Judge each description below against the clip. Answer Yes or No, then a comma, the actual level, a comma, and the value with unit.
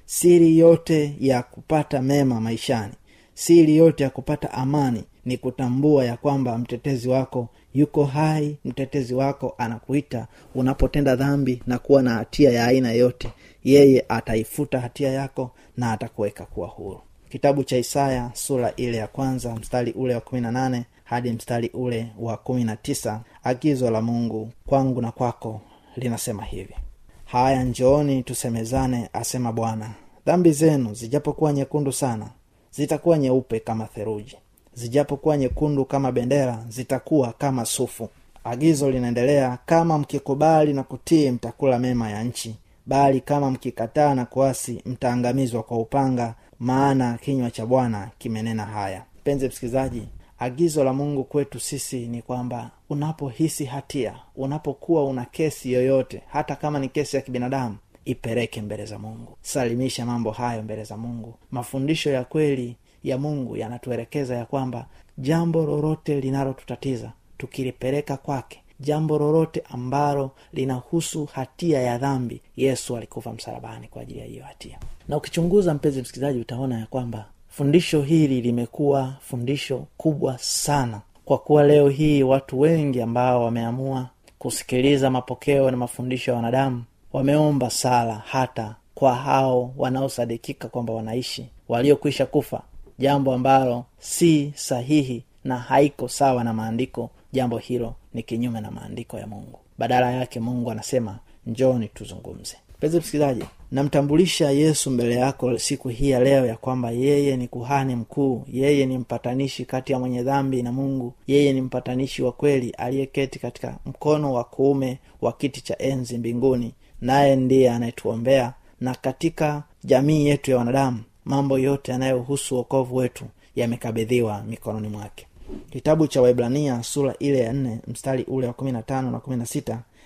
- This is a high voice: No, low, 130 Hz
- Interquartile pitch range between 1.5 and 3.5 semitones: Yes, average, 2.8 semitones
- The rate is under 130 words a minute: No, average, 135 wpm